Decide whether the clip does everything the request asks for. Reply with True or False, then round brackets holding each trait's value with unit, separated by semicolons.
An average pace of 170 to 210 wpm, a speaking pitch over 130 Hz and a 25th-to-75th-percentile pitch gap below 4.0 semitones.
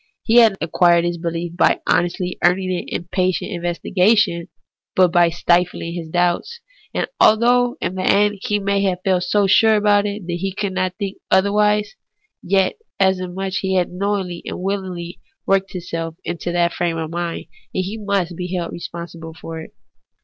True (180 wpm; 185 Hz; 2.5 semitones)